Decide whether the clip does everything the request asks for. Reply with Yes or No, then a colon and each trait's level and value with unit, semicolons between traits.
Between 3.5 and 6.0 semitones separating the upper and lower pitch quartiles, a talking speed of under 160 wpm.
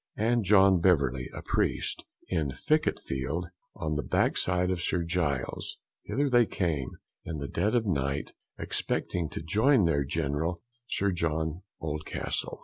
Yes: average, 4.5 semitones; average, 145 wpm